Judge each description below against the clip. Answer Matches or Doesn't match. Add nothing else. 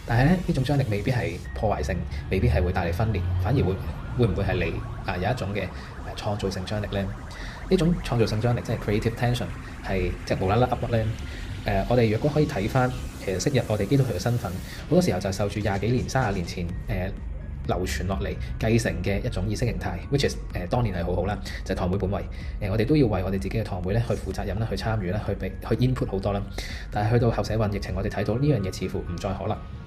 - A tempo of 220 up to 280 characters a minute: Doesn't match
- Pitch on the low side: Matches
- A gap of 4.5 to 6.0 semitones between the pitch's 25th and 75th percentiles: Doesn't match